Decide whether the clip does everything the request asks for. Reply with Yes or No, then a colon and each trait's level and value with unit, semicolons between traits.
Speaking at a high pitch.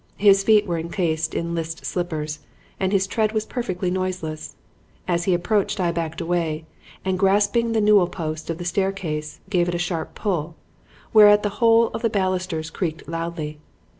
No: medium, 180 Hz